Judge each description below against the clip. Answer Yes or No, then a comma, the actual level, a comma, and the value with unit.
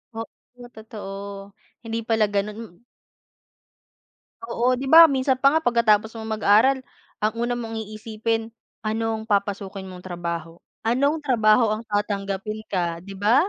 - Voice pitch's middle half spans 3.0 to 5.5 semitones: No, narrow, 2.4 semitones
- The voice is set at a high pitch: Yes, high, 215 Hz